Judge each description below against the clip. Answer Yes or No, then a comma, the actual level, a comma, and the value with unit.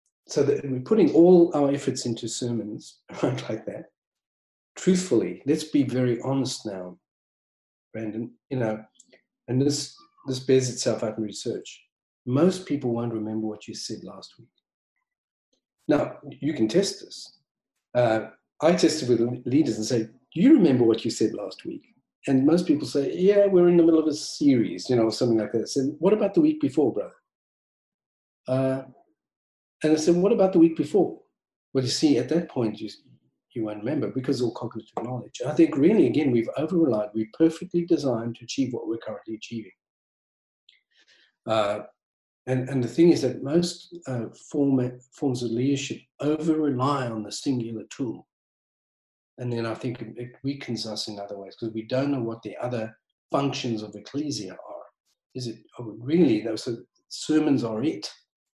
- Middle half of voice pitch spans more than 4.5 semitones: Yes, average, 5.2 semitones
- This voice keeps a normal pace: Yes, average, 180 wpm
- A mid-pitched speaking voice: No, low, 130 Hz